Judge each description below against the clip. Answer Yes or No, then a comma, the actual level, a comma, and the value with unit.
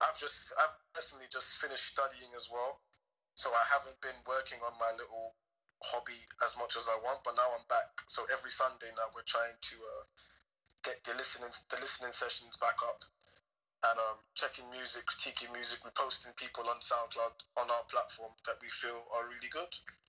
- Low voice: Yes, low, 120 Hz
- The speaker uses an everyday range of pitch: No, narrow, 2.3 semitones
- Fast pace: No, average, 185 wpm